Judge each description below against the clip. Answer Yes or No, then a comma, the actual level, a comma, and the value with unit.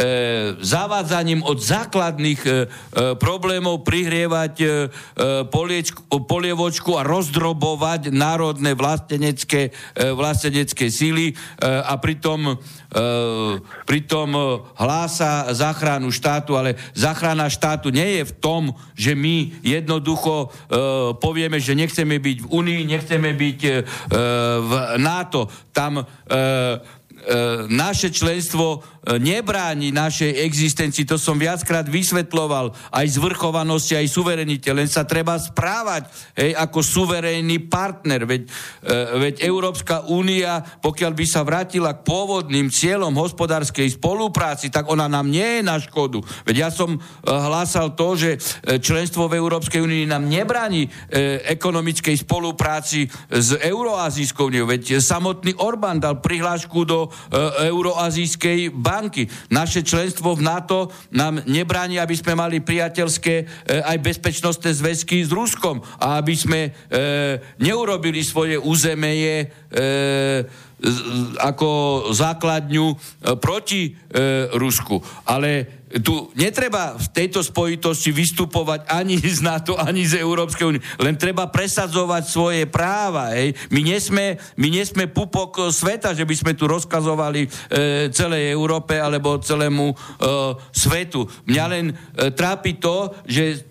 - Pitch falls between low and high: Yes, medium, 155 Hz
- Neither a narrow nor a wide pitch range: Yes, average, 3.3 semitones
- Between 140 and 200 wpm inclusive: No, average, 120 wpm